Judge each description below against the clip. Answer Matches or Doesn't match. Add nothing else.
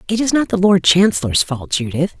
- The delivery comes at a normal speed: Doesn't match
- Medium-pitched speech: Matches